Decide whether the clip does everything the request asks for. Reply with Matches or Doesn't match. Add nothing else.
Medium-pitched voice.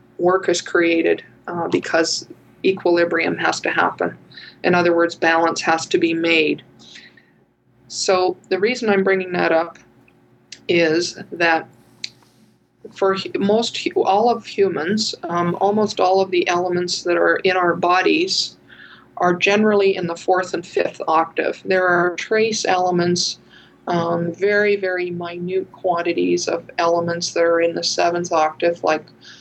Matches